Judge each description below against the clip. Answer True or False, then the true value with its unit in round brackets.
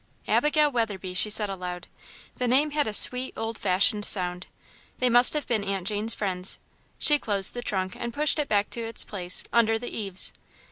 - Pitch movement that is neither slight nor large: True (4.1 semitones)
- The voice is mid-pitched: False (215 Hz)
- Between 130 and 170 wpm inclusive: False (190 wpm)